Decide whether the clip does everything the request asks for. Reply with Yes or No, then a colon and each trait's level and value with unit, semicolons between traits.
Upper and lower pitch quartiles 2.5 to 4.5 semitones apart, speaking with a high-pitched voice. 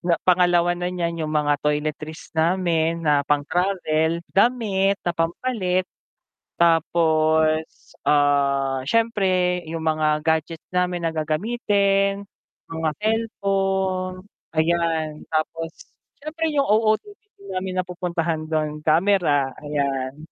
No: average, 3.6 semitones; medium, 170 Hz